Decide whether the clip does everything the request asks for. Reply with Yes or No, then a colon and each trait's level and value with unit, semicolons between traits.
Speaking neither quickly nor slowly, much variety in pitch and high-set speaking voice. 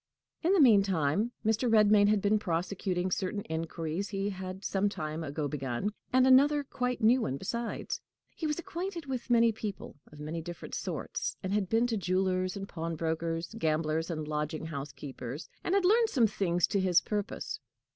Yes: average, 175 wpm; wide, 5.8 semitones; high, 195 Hz